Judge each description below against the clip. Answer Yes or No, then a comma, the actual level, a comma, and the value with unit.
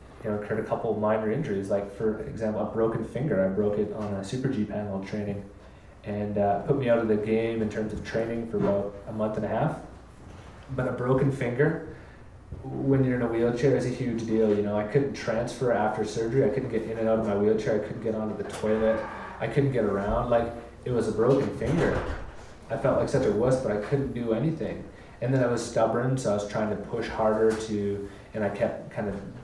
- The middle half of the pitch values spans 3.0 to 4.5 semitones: No, narrow, 2.4 semitones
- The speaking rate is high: Yes, fast, 235 wpm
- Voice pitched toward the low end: Yes, low, 110 Hz